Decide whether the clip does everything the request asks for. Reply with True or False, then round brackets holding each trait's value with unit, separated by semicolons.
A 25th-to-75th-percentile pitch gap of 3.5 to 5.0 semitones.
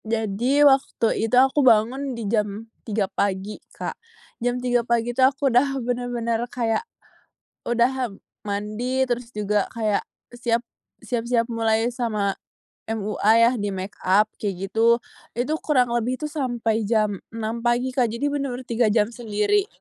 False (2.5 semitones)